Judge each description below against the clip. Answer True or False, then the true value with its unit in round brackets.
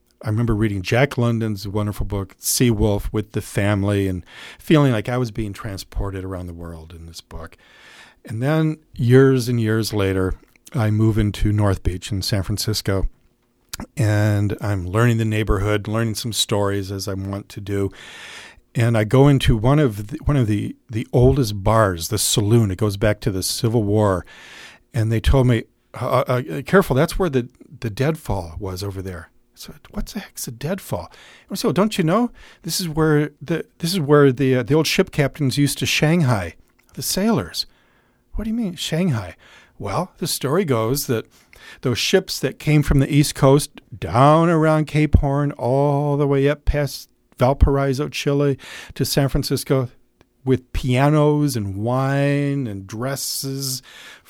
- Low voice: True (120 Hz)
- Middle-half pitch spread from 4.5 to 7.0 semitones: True (5.3 semitones)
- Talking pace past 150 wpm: True (170 wpm)